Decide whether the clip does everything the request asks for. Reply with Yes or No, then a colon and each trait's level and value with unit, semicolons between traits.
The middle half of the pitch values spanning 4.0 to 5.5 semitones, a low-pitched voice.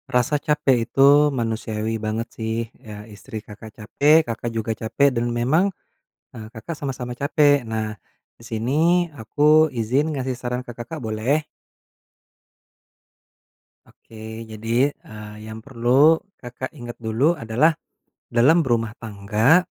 Yes: average, 4.3 semitones; low, 120 Hz